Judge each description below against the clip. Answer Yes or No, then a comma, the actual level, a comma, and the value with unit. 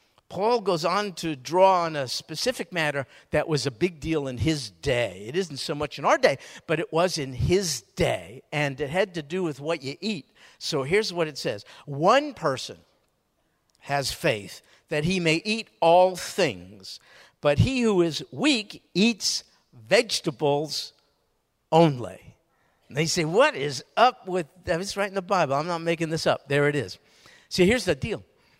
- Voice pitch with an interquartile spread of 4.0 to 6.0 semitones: Yes, average, 4.4 semitones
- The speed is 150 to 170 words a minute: No, average, 185 wpm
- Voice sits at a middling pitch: Yes, medium, 165 Hz